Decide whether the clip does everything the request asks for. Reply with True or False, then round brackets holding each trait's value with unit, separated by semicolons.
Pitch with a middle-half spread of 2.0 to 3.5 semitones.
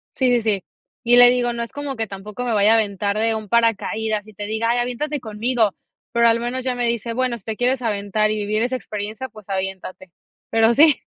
True (2.6 semitones)